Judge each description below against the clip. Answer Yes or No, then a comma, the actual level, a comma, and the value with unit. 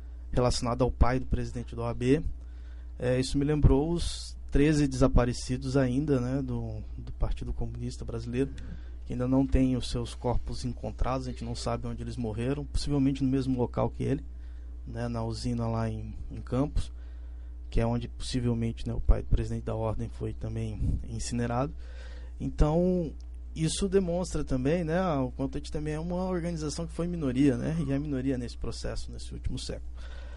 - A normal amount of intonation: No, wide, 8.3 semitones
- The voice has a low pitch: Yes, low, 120 Hz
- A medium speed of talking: Yes, average, 175 wpm